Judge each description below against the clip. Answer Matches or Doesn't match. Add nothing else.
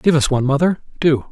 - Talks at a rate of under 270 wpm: Matches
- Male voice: Matches